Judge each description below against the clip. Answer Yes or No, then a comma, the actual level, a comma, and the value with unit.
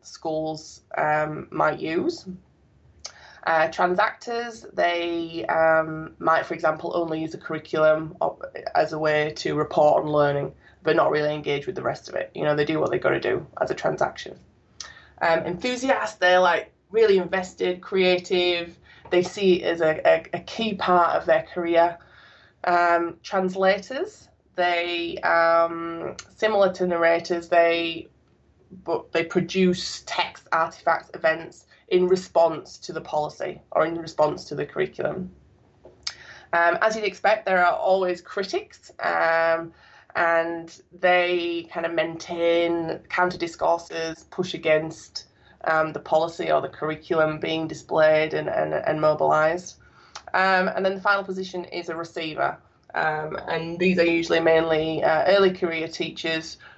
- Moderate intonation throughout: No, narrow, 2.1 semitones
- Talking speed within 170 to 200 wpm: No, average, 145 wpm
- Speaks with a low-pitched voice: No, medium, 170 Hz